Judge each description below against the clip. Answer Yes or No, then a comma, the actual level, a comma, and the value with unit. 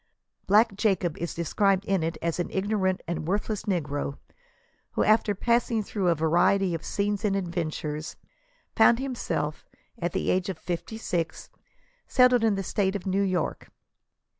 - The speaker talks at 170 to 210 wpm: No, average, 160 wpm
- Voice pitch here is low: No, high, 190 Hz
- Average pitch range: Yes, average, 3.4 semitones